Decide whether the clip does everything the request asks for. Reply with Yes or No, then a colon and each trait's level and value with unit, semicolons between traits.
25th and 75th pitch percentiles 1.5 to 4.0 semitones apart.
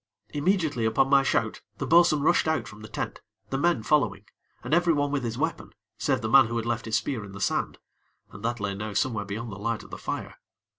No: average, 5.1 semitones